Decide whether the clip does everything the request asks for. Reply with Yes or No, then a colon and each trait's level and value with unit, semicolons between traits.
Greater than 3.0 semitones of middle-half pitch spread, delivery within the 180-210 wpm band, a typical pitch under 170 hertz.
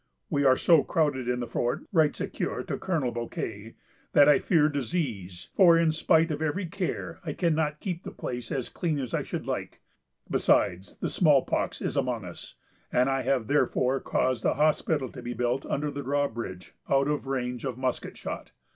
Yes: average, 4.1 semitones; average, 190 wpm; low, 135 Hz